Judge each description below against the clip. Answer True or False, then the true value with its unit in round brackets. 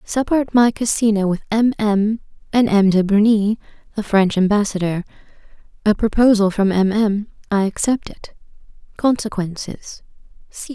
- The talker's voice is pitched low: False (210 Hz)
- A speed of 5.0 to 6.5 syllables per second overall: False (4.7 syllables/s)